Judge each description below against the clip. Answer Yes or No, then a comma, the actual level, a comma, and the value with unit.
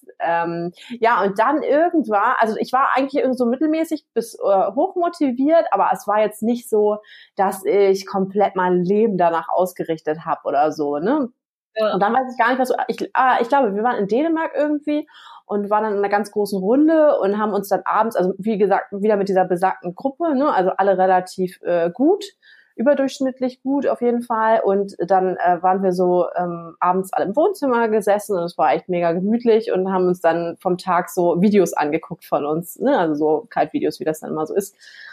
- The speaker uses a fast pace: Yes, fast, 205 wpm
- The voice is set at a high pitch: Yes, high, 205 Hz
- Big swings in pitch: Yes, wide, 6.1 semitones